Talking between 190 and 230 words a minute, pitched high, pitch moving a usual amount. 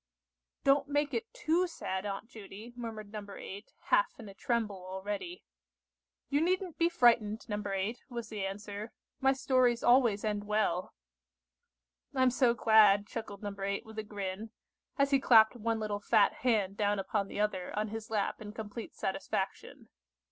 No: average, 160 wpm; high, 215 Hz; average, 3.3 semitones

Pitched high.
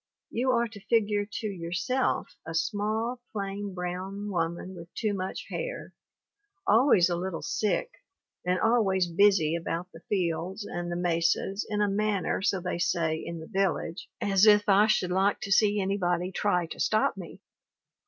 Yes: high, 195 Hz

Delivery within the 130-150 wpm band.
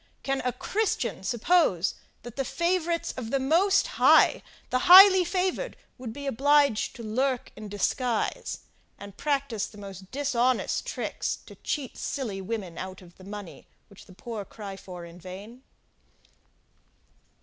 Yes: average, 145 wpm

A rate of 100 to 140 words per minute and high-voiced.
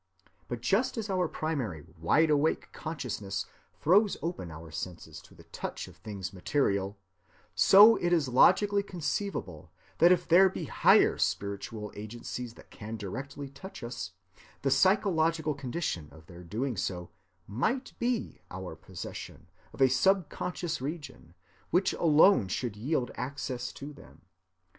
No: slow, 135 wpm; low, 135 Hz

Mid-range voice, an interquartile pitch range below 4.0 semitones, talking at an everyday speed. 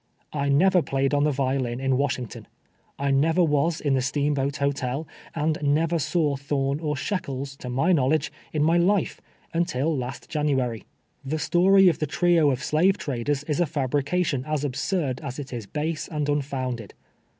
Yes: medium, 145 Hz; average, 2.9 semitones; average, 175 wpm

